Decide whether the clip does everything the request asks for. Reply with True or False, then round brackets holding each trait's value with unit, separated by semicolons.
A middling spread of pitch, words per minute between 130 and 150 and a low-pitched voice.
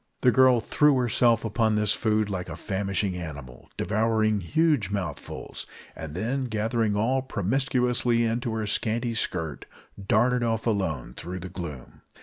True (4.1 semitones; 140 wpm; 110 Hz)